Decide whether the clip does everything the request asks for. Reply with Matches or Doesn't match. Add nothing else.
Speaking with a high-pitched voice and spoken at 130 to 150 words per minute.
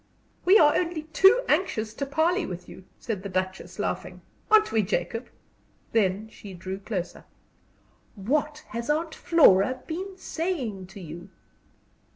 Matches